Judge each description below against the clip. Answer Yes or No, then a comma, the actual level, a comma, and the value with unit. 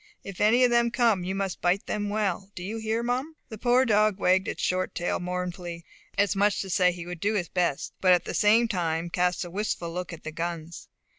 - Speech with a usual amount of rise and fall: Yes, average, 3.4 semitones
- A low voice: No, high, 190 Hz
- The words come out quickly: Yes, fast, 235 wpm